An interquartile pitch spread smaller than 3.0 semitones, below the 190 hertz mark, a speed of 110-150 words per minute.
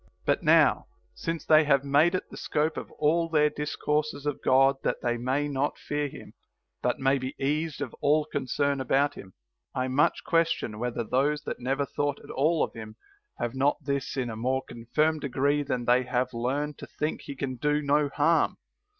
No: narrow, 2.5 semitones; medium, 140 Hz; average, 195 wpm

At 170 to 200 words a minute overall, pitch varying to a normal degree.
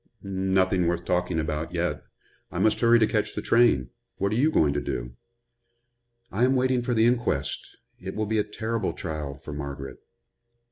No: average, 180 wpm; wide, 6.8 semitones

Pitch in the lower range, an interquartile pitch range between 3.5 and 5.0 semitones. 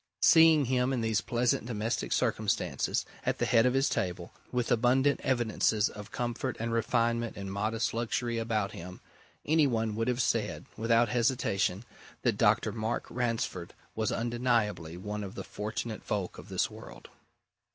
No: low, 115 Hz; narrow, 2.5 semitones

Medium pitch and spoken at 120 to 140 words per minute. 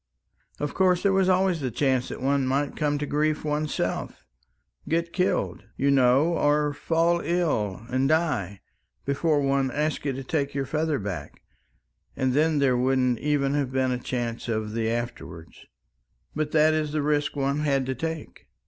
No: medium, 145 Hz; average, 170 wpm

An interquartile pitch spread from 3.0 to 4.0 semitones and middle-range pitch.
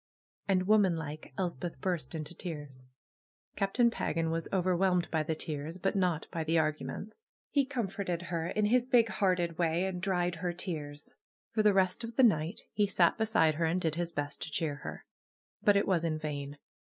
Yes: average, 3.5 semitones; medium, 175 Hz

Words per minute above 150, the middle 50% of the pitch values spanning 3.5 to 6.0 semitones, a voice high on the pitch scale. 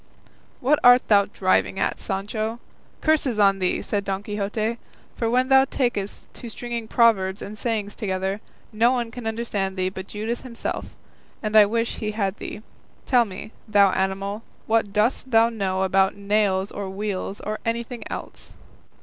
No: average, 160 wpm; average, 2.9 semitones; high, 215 Hz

